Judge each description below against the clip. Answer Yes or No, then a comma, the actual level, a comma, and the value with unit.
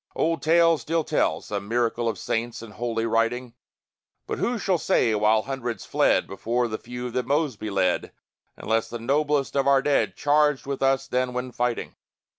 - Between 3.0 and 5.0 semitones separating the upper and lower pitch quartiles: Yes, average, 3.7 semitones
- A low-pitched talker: Yes, low, 125 Hz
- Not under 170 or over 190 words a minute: Yes, average, 175 wpm